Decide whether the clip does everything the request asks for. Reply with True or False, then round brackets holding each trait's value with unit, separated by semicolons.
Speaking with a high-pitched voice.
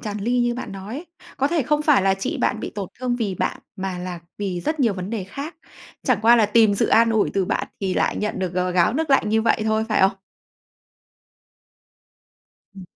True (215 Hz)